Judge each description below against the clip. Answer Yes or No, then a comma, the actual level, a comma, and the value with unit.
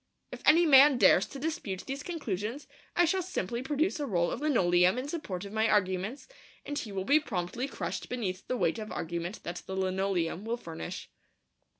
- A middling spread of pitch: No, wide, 7.5 semitones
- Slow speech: No, average, 190 wpm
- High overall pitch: Yes, high, 220 Hz